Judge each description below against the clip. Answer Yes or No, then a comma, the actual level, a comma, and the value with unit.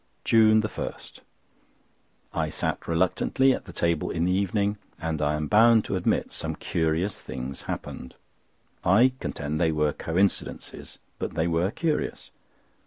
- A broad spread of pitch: No, average, 4.9 semitones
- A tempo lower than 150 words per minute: Yes, slow, 135 wpm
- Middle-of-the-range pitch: No, very low, 85 Hz